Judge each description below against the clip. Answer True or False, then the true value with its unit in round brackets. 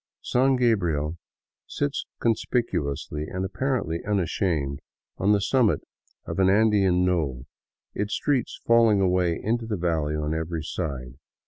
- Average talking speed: False (125 wpm)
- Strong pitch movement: True (5.8 semitones)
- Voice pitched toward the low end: True (95 Hz)